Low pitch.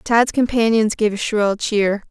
No: high, 215 Hz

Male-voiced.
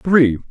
Yes: male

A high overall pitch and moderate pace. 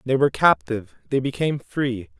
No: low, 135 Hz; average, 165 wpm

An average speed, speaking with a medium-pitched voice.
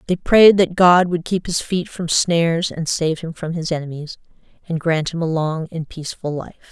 No: fast, 215 wpm; medium, 165 Hz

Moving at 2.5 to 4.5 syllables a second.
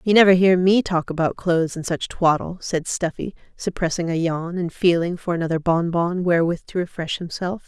No: 5.3 syllables/s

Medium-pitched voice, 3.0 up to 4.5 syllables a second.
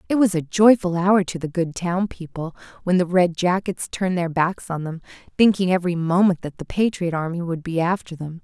No: medium, 180 Hz; 5.4 syllables/s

